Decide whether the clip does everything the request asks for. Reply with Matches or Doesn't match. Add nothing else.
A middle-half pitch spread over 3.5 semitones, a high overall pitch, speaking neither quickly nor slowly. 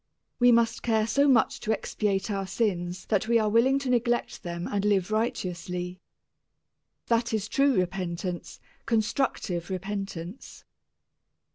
Doesn't match